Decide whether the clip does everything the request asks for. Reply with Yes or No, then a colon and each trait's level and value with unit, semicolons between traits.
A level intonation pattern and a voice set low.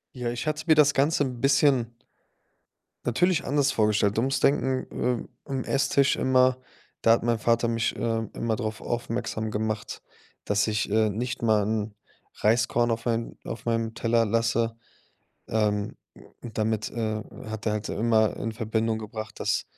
Yes: narrow, 2.3 semitones; low, 115 Hz